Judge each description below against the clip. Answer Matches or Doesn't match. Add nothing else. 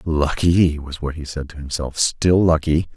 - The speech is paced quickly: Doesn't match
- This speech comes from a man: Matches